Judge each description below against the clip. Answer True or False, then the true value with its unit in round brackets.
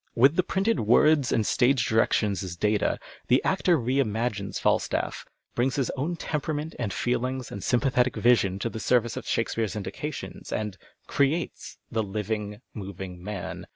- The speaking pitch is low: True (120 Hz)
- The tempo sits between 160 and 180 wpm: True (170 wpm)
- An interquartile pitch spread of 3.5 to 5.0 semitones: True (4.5 semitones)